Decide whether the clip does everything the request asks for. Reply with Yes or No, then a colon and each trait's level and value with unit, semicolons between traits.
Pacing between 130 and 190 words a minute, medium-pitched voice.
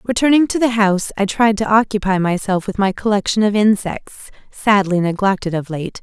No: average, 180 wpm; high, 205 Hz